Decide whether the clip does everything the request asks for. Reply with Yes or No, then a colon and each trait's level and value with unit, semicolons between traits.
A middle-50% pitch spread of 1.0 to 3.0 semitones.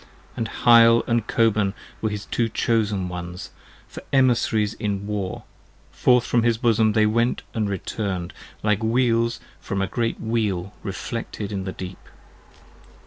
Yes: average, 2.7 semitones